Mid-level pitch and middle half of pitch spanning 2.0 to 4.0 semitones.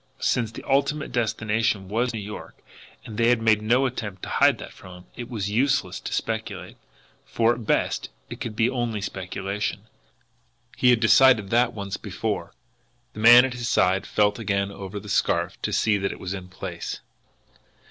No: low, 110 Hz; average, 3.2 semitones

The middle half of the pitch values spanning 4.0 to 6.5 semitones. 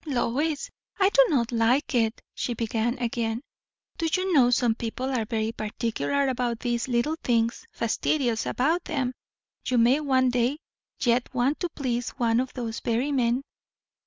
No: average, 2.8 semitones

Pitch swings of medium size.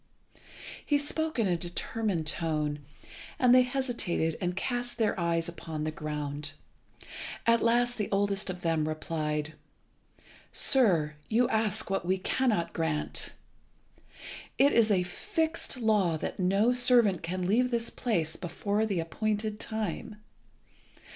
No: wide, 6.0 semitones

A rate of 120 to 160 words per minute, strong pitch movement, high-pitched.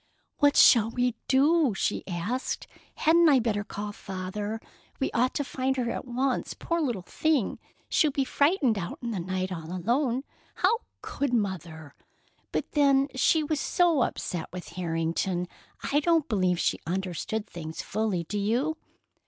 Yes: average, 155 wpm; wide, 7.2 semitones; high, 230 Hz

